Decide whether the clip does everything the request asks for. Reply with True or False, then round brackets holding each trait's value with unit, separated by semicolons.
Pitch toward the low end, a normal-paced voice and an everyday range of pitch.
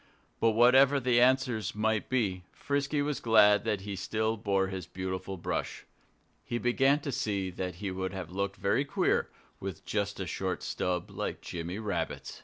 True (105 Hz; 170 wpm; 4.4 semitones)